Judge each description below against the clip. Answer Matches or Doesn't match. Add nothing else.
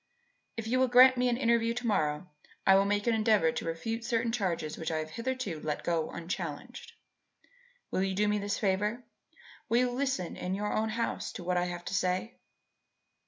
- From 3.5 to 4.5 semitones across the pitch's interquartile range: Doesn't match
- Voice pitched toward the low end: Doesn't match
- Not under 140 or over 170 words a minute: Doesn't match